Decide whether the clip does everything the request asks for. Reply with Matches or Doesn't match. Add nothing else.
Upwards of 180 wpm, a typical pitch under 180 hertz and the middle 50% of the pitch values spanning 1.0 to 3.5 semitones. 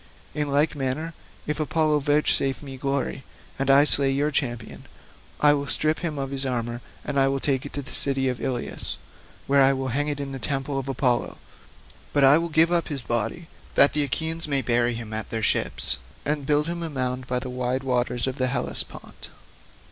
Matches